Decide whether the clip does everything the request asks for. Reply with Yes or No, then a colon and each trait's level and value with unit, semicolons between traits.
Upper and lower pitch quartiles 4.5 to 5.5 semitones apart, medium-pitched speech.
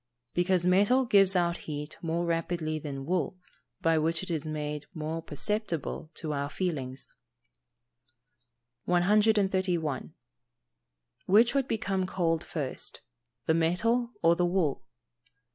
No: average, 3.5 semitones; medium, 170 Hz